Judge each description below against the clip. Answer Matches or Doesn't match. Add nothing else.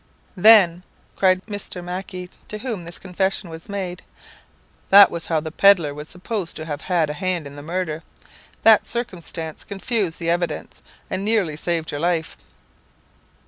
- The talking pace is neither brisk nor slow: Matches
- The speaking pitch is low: Doesn't match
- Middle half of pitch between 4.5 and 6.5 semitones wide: Doesn't match